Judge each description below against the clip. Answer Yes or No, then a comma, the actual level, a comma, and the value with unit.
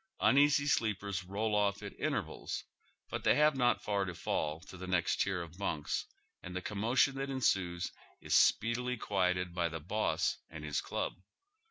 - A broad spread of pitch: No, average, 4.8 semitones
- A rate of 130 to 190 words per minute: Yes, average, 170 wpm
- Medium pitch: No, low, 100 Hz